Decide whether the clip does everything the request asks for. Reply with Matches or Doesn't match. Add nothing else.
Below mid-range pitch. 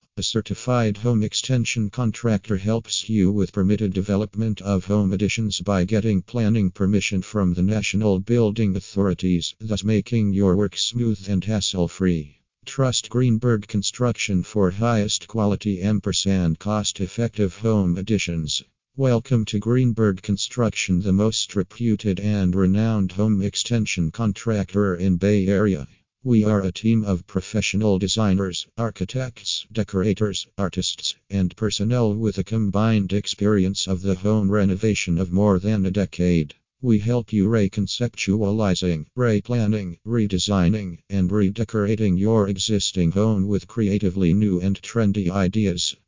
Matches